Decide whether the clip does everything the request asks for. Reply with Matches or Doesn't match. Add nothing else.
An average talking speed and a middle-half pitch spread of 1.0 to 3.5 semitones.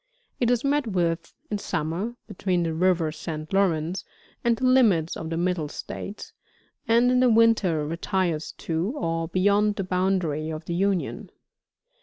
Doesn't match